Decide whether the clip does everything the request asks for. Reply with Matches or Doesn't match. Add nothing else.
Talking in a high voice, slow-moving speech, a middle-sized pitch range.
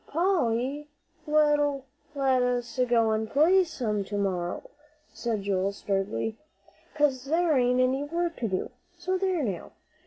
Doesn't match